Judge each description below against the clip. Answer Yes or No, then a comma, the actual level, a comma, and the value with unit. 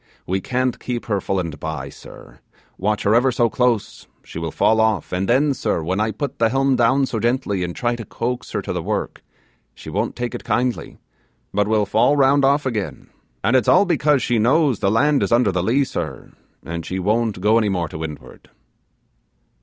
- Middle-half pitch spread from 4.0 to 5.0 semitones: Yes, average, 4.7 semitones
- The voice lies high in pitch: No, low, 115 Hz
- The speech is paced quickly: Yes, fast, 210 wpm